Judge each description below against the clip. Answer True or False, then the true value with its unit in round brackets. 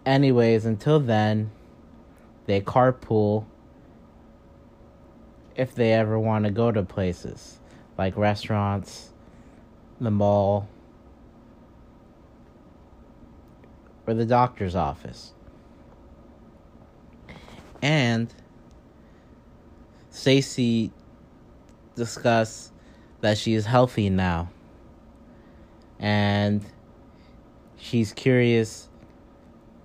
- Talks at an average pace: False (65 wpm)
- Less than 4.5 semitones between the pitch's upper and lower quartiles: True (2.5 semitones)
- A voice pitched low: True (110 Hz)